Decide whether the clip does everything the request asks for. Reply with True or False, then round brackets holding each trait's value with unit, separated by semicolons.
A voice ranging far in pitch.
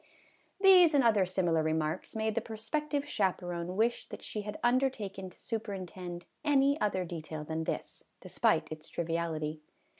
True (5.9 semitones)